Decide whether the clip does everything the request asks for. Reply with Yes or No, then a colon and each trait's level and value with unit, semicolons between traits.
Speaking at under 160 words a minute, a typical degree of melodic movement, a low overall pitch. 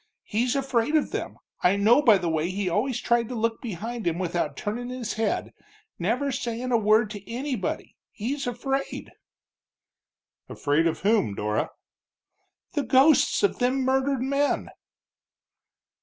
No: average, 140 wpm; average, 4.5 semitones; high, 235 Hz